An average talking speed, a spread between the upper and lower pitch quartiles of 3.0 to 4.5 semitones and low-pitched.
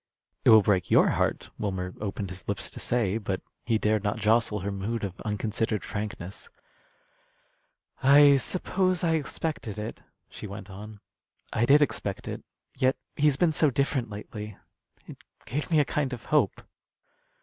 No: average, 160 wpm; average, 5.2 semitones; low, 110 Hz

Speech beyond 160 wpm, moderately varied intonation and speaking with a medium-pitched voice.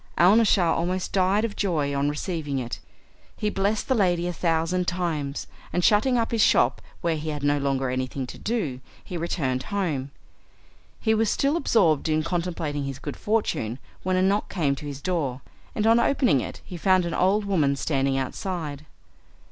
No: average, 180 wpm; wide, 5.7 semitones; medium, 170 Hz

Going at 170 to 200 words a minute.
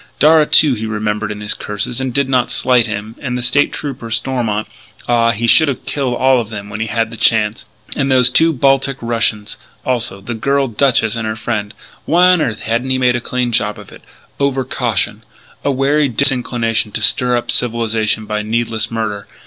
Yes: average, 195 wpm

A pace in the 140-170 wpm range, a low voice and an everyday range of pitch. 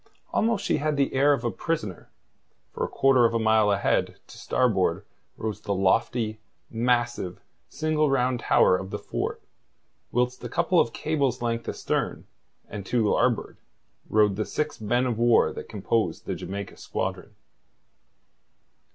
Yes: average, 150 wpm; low, 120 Hz; average, 3.8 semitones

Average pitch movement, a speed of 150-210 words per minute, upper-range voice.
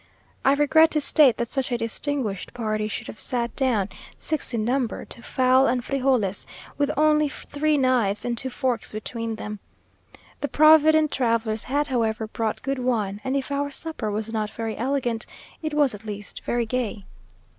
Yes: average, 4.2 semitones; average, 175 wpm; high, 245 Hz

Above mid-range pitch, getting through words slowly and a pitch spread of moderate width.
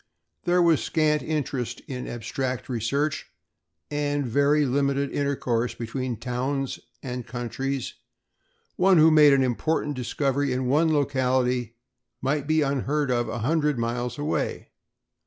No: low, 135 Hz; slow, 125 wpm; average, 3.0 semitones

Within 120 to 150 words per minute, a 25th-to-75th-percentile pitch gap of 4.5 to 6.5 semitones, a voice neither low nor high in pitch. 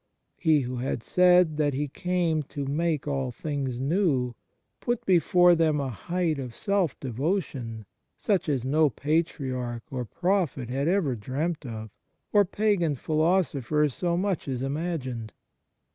Yes: average, 140 wpm; average, 5.1 semitones; medium, 150 Hz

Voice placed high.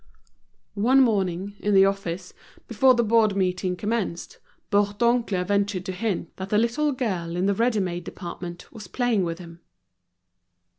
Yes: high, 200 Hz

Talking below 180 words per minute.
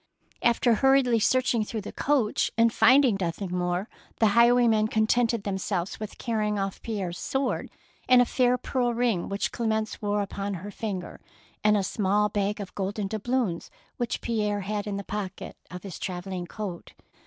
Yes: average, 165 wpm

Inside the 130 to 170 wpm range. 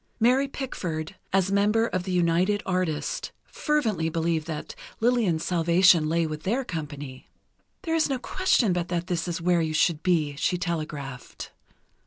Yes: average, 150 wpm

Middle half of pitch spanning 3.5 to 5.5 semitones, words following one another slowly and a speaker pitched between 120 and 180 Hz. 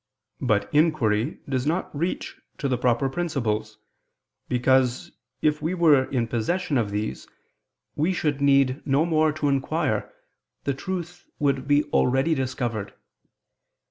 Yes: average, 3.8 semitones; slow, 130 wpm; medium, 140 Hz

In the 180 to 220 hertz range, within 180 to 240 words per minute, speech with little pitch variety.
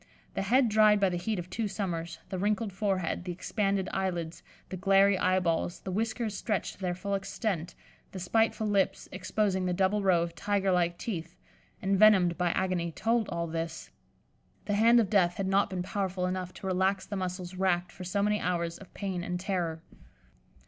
Yes: high, 190 Hz; average, 185 wpm; narrow, 2.2 semitones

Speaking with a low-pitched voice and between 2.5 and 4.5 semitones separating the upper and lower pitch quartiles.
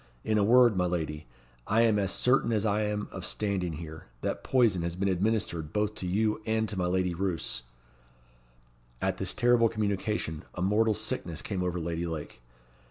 Yes: low, 100 Hz; average, 3.8 semitones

